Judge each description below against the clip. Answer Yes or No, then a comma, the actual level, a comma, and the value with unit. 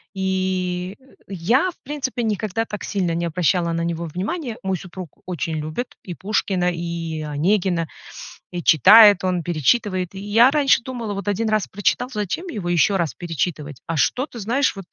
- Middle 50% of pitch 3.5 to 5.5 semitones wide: Yes, average, 4.2 semitones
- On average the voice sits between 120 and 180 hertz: No, high, 190 Hz